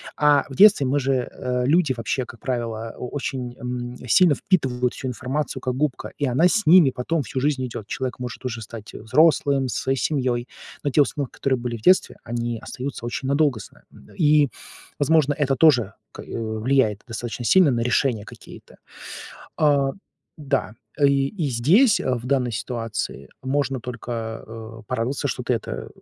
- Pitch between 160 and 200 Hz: No, low, 130 Hz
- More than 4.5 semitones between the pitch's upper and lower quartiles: No, average, 3.2 semitones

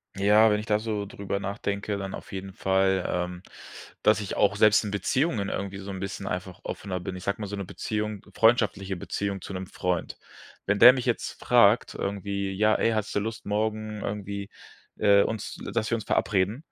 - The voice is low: Yes, low, 100 Hz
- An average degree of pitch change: No, narrow, 1.8 semitones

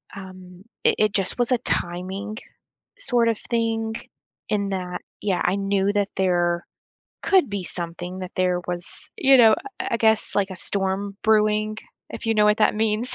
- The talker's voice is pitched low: No, high, 200 Hz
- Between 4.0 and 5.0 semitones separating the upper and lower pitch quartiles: No, average, 3.0 semitones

